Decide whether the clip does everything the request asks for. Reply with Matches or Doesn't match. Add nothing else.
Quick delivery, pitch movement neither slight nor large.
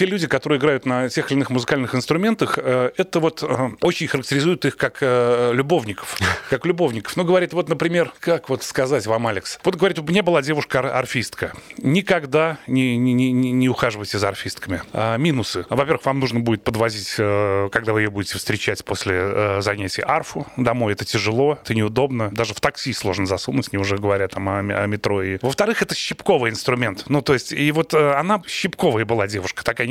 Doesn't match